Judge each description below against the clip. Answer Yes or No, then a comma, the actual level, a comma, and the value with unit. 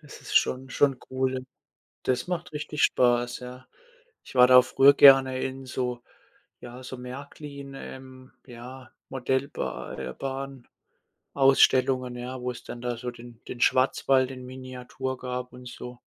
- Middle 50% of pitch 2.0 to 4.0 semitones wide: No, narrow, 1.2 semitones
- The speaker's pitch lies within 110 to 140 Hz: Yes, low, 130 Hz